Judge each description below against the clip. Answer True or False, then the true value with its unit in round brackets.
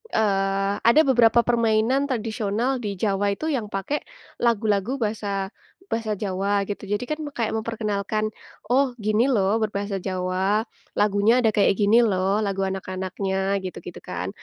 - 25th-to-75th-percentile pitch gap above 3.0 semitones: False (2.6 semitones)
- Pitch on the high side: True (210 Hz)